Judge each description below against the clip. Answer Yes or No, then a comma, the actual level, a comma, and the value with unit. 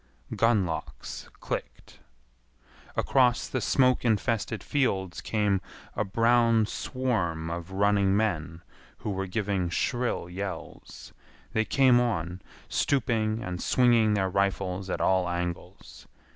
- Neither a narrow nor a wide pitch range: Yes, average, 4.2 semitones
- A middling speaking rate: No, slow, 115 wpm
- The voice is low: Yes, low, 100 Hz